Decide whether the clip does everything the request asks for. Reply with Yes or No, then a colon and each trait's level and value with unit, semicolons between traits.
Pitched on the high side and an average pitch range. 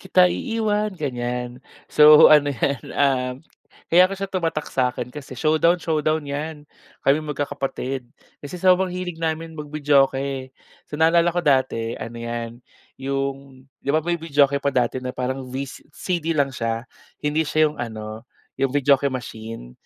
No: medium, 140 Hz; average, 3.7 semitones